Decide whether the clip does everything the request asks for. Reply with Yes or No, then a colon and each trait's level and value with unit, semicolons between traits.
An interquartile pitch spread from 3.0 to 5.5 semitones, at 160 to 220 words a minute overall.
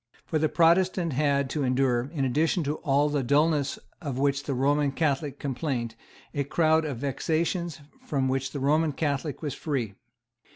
No: narrow, 2.6 semitones; average, 165 wpm